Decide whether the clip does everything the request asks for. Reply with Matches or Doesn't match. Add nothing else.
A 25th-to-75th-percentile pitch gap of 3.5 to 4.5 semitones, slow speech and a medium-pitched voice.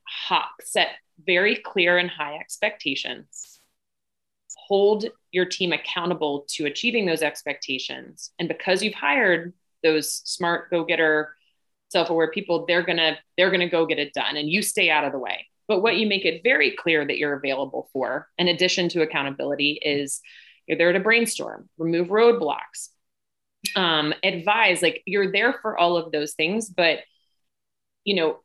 Doesn't match